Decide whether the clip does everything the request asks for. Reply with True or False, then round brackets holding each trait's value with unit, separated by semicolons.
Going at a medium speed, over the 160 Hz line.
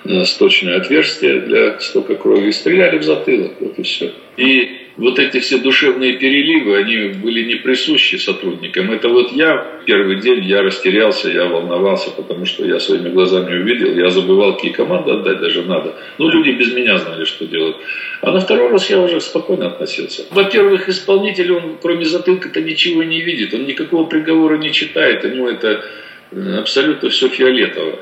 False (170 wpm; 190 Hz)